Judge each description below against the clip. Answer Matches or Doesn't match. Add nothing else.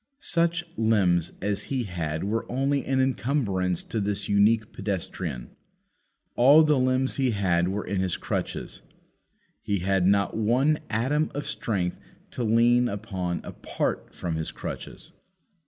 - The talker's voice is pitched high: Doesn't match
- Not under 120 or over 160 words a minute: Matches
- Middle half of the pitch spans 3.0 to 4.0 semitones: Doesn't match